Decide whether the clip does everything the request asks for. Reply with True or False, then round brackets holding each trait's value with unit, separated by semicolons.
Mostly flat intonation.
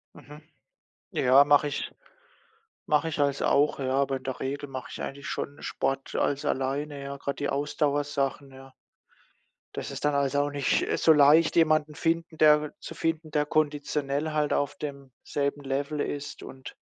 True (1.5 semitones)